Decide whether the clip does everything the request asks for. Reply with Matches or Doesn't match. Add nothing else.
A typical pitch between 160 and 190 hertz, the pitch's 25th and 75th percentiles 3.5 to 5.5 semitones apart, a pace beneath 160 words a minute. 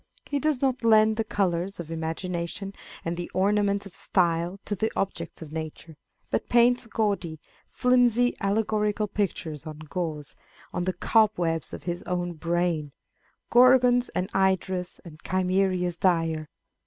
Matches